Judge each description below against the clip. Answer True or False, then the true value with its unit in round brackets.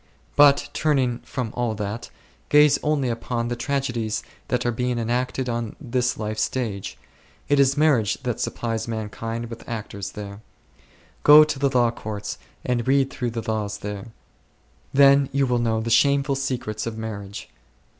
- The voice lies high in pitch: False (120 Hz)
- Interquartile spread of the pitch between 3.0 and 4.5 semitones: True (3.5 semitones)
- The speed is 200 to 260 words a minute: False (155 wpm)